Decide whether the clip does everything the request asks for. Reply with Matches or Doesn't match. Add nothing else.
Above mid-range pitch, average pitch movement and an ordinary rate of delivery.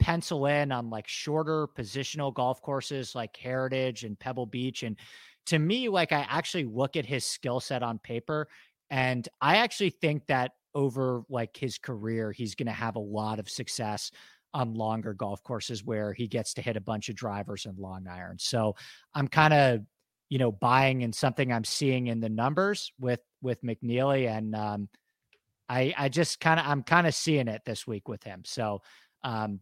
Doesn't match